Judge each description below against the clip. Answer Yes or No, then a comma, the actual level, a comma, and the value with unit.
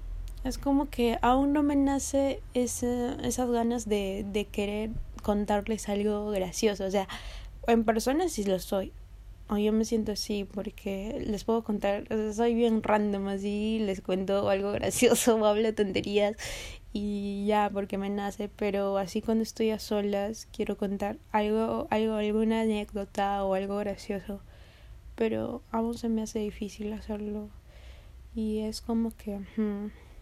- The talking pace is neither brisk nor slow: Yes, average, 155 wpm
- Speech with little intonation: Yes, narrow, 1.9 semitones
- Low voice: No, high, 210 Hz